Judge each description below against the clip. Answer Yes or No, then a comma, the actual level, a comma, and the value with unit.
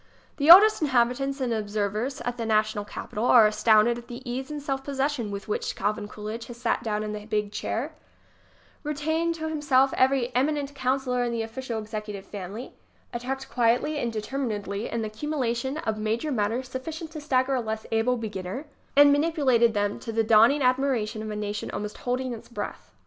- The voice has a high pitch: Yes, high, 240 Hz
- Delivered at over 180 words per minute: Yes, average, 190 wpm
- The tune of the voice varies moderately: Yes, average, 4.0 semitones